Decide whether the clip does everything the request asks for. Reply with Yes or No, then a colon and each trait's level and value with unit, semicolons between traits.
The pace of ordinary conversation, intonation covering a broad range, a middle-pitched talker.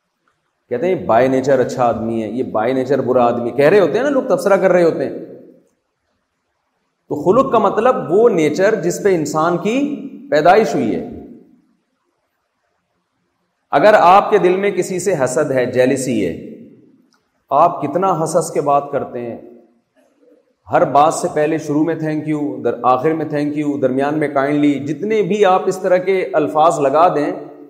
Yes: average, 170 wpm; wide, 6.0 semitones; medium, 155 Hz